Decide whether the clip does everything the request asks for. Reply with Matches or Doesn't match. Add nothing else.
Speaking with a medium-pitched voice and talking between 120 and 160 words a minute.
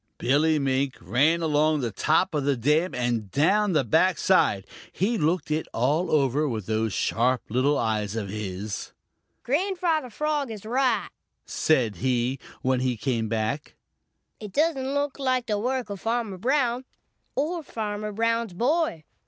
Matches